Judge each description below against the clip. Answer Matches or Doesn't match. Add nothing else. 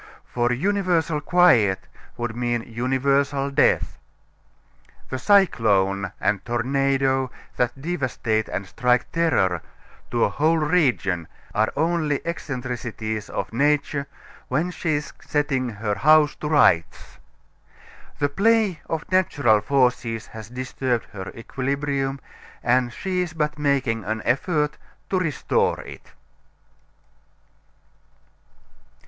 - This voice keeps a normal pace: Doesn't match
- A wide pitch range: Doesn't match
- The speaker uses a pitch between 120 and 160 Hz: Matches